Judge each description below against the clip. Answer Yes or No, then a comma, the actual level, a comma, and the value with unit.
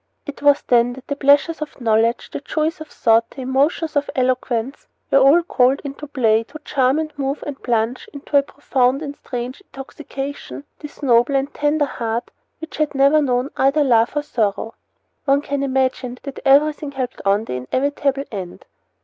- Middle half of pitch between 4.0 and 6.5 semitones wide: No, average, 2.8 semitones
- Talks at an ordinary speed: Yes, average, 175 wpm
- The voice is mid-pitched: No, very high, 275 Hz